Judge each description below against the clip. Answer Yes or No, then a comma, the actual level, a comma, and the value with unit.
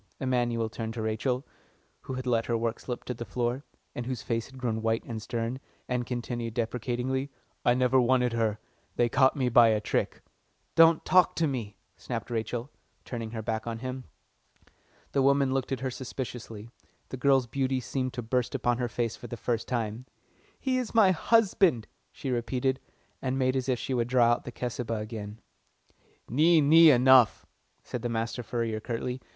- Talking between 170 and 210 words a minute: Yes, average, 180 wpm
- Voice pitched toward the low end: Yes, low, 125 Hz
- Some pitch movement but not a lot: No, narrow, 2.3 semitones